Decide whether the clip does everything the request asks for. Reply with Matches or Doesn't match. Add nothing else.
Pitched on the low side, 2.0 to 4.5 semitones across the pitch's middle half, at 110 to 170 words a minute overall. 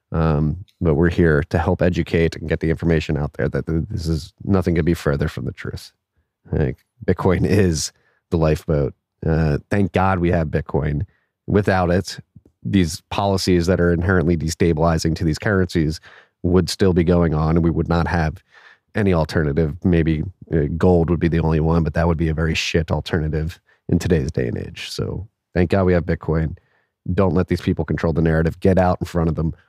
Doesn't match